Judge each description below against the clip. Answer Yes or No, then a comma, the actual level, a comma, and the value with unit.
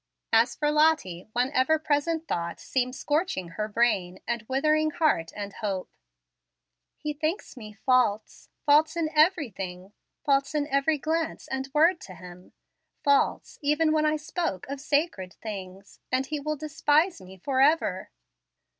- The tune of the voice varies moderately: No, wide, 6.9 semitones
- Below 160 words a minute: Yes, average, 145 wpm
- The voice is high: Yes, very high, 275 Hz